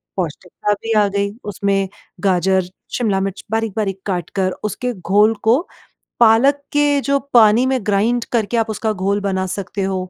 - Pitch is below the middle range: No, high, 205 Hz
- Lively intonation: No, average, 2.9 semitones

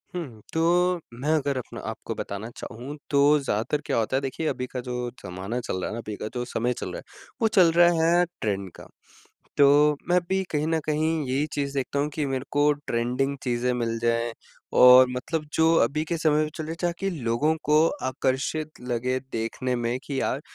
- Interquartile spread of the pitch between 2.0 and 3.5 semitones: No, average, 4.3 semitones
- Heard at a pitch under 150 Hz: Yes, low, 135 Hz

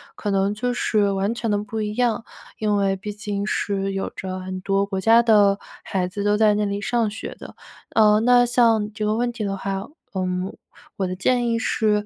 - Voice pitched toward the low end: No, high, 210 Hz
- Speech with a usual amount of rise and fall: No, narrow, 2.1 semitones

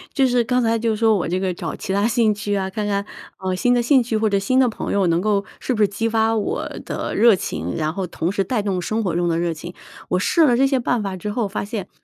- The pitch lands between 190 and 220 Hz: Yes, high, 210 Hz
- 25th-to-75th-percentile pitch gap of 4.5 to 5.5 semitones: No, average, 3.6 semitones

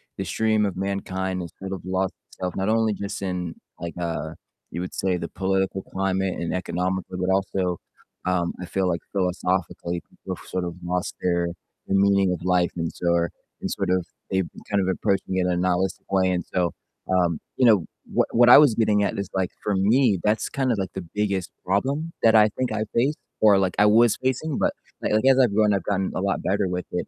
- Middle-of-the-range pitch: No, very low, 95 Hz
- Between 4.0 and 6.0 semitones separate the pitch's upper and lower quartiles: No, narrow, 2.5 semitones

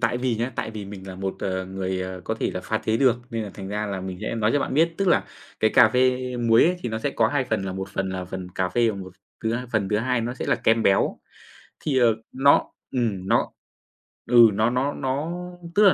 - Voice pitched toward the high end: No, low, 110 Hz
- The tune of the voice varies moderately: Yes, average, 4.7 semitones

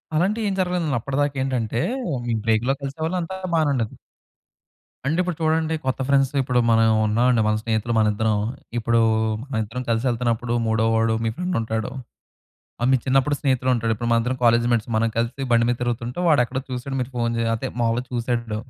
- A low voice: Yes, low, 120 Hz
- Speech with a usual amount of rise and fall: Yes, average, 3.1 semitones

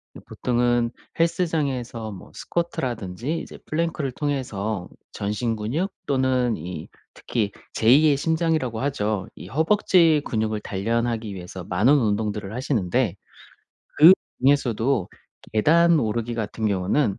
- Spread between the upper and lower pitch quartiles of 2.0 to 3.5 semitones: No, wide, 5.4 semitones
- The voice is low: Yes, low, 120 Hz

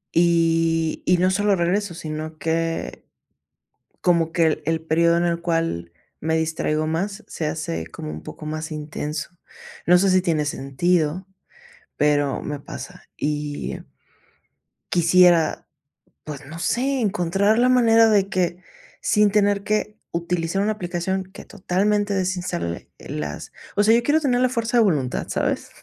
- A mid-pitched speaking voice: Yes, medium, 170 Hz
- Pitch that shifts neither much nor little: Yes, average, 4.1 semitones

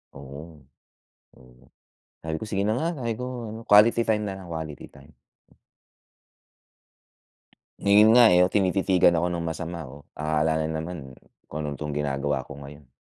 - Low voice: Yes, very low, 80 Hz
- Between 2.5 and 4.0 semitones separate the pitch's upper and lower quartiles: No, wide, 5.5 semitones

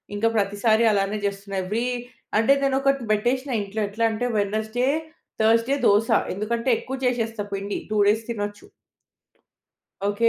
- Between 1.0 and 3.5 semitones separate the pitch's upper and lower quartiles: Yes, average, 2.7 semitones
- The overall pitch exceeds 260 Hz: No, high, 220 Hz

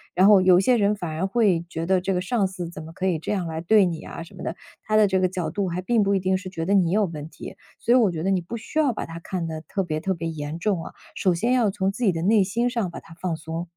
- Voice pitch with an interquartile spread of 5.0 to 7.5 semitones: No, average, 3.5 semitones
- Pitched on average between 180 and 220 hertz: Yes, medium, 185 Hz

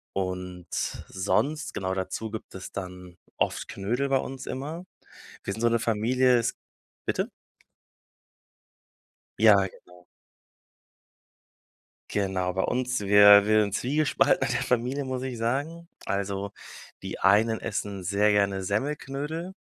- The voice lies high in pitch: No, low, 105 Hz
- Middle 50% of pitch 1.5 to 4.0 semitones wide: No, average, 4.9 semitones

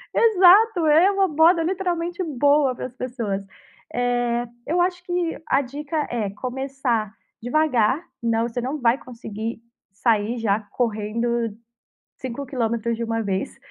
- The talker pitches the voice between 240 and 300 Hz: Yes, very high, 250 Hz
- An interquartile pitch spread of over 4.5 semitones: Yes, wide, 5.6 semitones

